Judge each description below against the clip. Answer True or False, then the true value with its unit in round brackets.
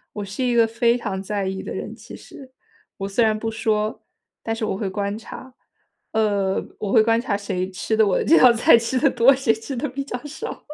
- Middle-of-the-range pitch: False (225 Hz)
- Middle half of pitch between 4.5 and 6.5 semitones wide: False (3.1 semitones)